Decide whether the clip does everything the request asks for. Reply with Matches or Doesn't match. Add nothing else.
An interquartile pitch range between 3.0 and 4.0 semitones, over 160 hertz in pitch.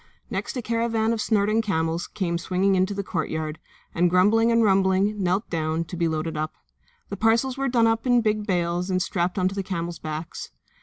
Doesn't match